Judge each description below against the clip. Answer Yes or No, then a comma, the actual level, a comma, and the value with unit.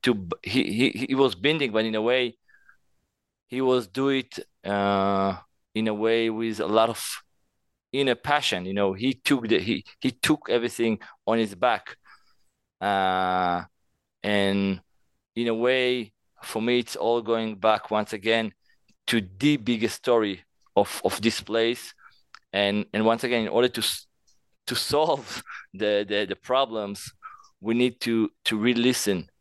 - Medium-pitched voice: No, low, 115 Hz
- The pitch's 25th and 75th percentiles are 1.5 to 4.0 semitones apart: Yes, average, 3.3 semitones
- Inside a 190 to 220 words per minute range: No, average, 155 wpm